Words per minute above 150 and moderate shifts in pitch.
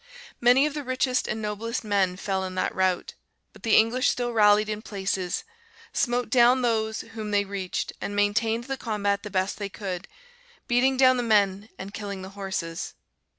Yes: average, 180 wpm; average, 3.5 semitones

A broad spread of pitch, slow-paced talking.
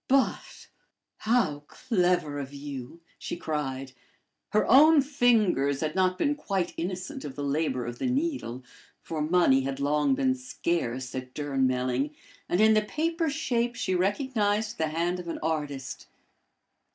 No: wide, 8.6 semitones; average, 145 wpm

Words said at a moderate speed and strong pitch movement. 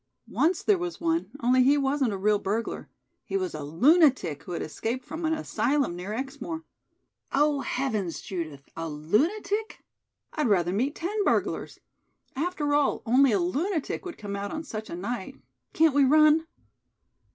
Yes: average, 165 wpm; wide, 7.9 semitones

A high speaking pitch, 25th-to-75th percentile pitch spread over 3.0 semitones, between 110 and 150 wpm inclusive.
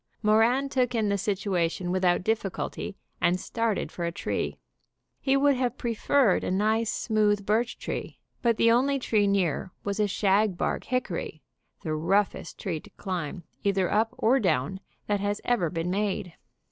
No: high, 205 Hz; average, 3.9 semitones; average, 160 wpm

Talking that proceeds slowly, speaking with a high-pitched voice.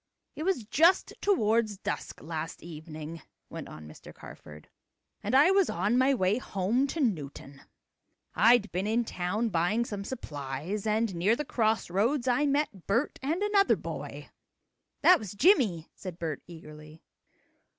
No: average, 150 wpm; high, 210 Hz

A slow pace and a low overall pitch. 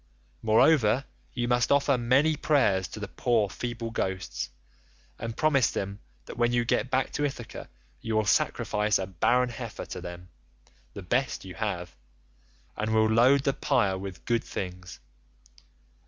No: average, 155 wpm; low, 115 Hz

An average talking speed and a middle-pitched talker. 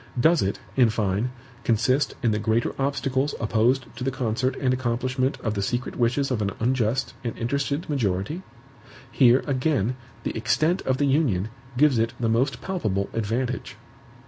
No: average, 160 wpm; low, 125 Hz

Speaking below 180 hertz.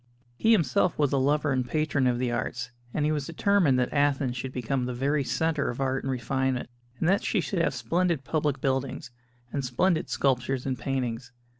Yes: low, 135 Hz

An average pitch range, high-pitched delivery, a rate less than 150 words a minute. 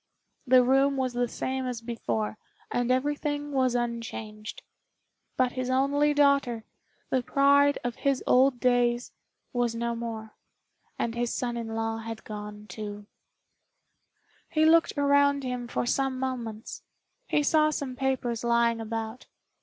Yes: average, 3.0 semitones; high, 245 Hz; average, 140 wpm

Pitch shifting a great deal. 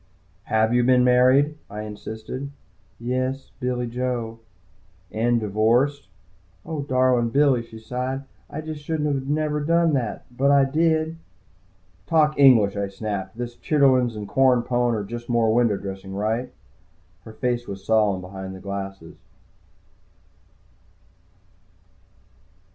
No: average, 3.8 semitones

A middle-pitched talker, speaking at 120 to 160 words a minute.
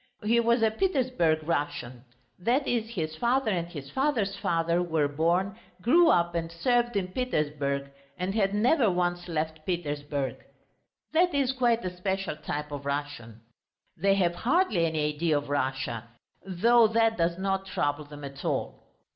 Yes: medium, 175 Hz; average, 155 wpm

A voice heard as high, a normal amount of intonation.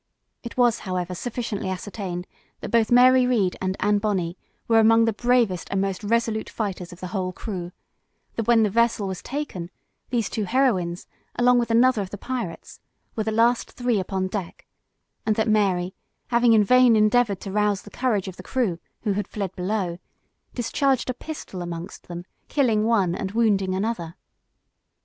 Yes: high, 210 Hz; average, 3.9 semitones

